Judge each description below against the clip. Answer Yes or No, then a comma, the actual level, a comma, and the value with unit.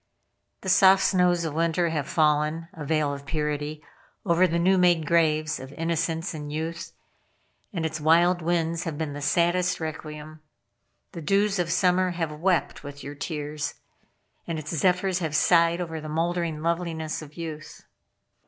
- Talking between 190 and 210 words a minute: No, average, 160 wpm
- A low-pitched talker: No, medium, 165 Hz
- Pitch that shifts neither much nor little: No, narrow, 2.2 semitones